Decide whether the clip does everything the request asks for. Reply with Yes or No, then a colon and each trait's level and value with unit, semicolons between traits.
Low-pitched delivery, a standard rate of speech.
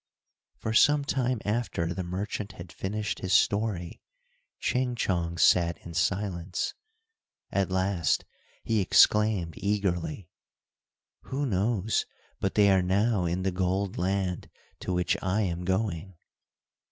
No: very low, 95 Hz; slow, 125 wpm